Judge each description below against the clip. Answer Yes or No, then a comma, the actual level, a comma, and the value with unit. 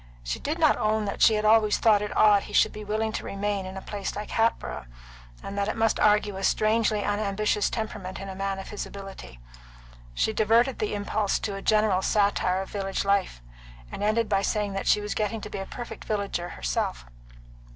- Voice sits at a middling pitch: No, high, 205 Hz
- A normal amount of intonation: No, narrow, 1.6 semitones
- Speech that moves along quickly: Yes, fast, 210 wpm